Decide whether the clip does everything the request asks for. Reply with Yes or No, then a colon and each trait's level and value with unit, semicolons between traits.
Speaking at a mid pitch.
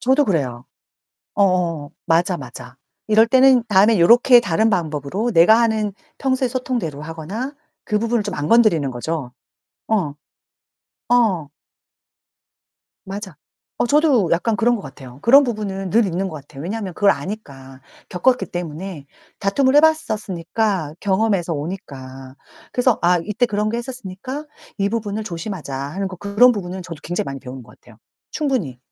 No: high, 195 Hz